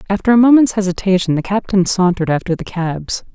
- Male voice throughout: No, female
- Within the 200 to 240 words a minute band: No, average, 180 wpm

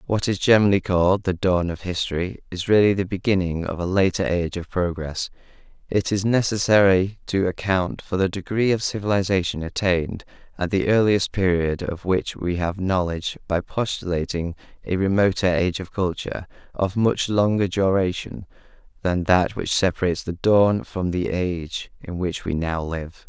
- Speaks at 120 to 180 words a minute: Yes, average, 160 wpm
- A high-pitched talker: No, very low, 95 Hz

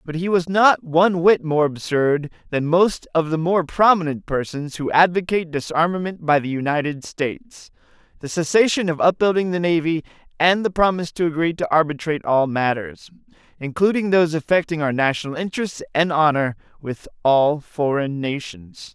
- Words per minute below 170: Yes, average, 160 wpm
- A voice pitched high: No, medium, 160 Hz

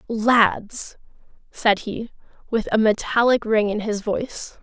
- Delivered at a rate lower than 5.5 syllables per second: Yes, 3.7 syllables/s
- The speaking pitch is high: Yes, high, 220 Hz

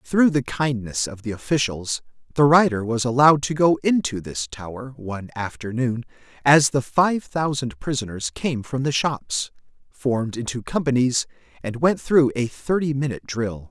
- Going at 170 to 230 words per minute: No, average, 160 wpm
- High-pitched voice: No, low, 130 Hz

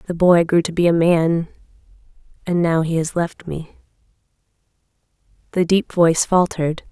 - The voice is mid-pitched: Yes, medium, 170 Hz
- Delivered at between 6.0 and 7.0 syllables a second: No, 4.9 syllables/s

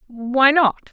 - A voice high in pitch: Yes, very high, 265 Hz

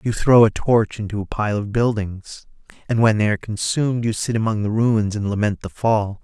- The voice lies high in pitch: No, low, 110 Hz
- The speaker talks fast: Yes, fast, 220 wpm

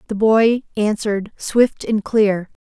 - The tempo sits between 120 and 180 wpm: Yes, slow, 135 wpm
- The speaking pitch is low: No, high, 215 Hz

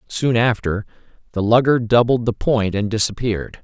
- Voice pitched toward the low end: Yes, low, 115 Hz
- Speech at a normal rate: Yes, average, 150 wpm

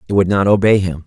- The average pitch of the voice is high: No, very low, 95 Hz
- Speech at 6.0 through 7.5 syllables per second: Yes, 6.7 syllables/s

